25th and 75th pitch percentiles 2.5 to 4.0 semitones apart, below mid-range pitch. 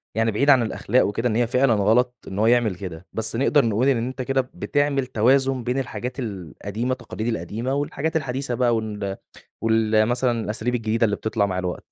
Yes: average, 3.0 semitones; low, 115 Hz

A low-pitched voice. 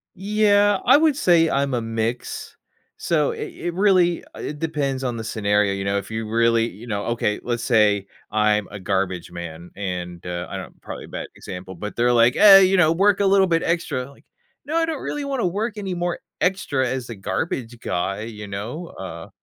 Yes: low, 120 Hz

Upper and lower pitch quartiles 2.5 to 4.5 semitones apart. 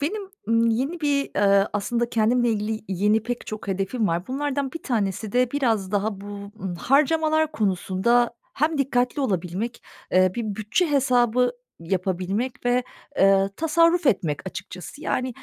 No: wide, 5.4 semitones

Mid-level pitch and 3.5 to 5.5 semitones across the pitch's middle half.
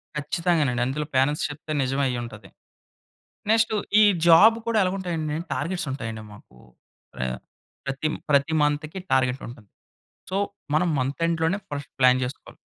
Yes: medium, 145 Hz; average, 4.5 semitones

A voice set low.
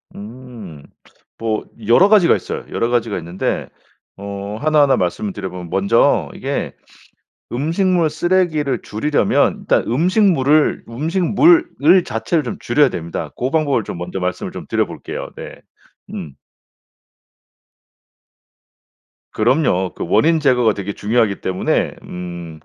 Yes: low, 120 Hz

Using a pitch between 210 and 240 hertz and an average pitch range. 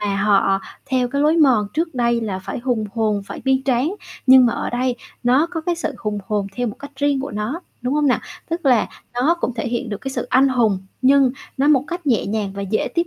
No: very high, 250 Hz; average, 4.6 semitones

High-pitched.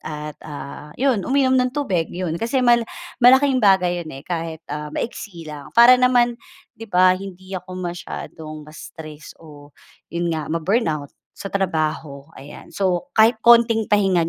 No: medium, 180 Hz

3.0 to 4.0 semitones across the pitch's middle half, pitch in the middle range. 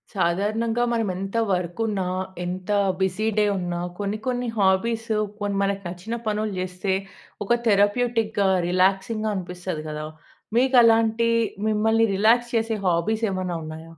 No: average, 3.5 semitones; high, 205 Hz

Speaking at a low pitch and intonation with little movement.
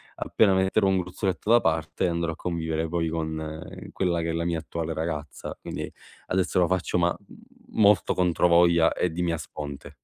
Yes: very low, 85 Hz; narrow, 1.9 semitones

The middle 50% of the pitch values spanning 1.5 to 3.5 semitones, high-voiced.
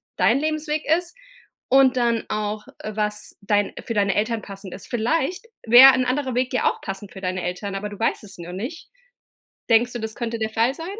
No: average, 4.2 semitones; high, 225 Hz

